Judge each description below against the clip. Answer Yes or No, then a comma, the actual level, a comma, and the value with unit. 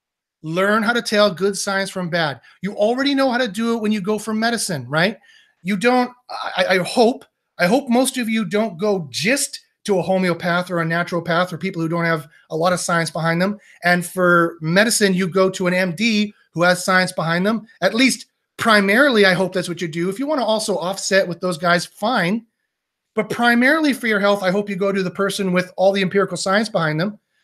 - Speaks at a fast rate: Yes, fast, 225 wpm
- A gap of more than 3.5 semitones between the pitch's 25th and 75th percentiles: Yes, average, 3.9 semitones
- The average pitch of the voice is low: No, high, 195 Hz